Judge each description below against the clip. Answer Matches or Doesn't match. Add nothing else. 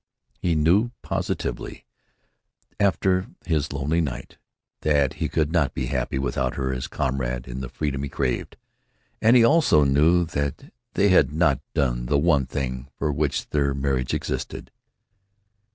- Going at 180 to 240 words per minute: Doesn't match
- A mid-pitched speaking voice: Doesn't match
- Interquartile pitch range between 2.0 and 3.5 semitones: Doesn't match